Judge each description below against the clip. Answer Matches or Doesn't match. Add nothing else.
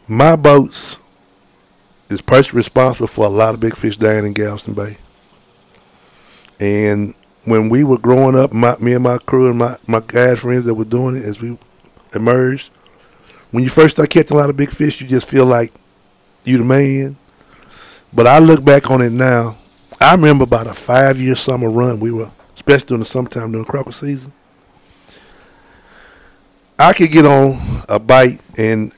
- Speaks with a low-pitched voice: Matches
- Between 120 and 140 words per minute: Doesn't match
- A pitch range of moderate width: Matches